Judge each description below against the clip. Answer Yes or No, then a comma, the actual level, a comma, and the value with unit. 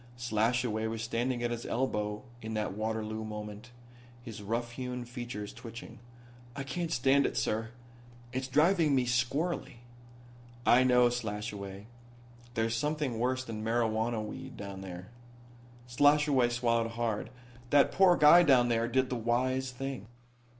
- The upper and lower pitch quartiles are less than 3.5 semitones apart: Yes, average, 2.8 semitones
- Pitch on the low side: Yes, low, 120 Hz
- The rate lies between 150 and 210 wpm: No, slow, 135 wpm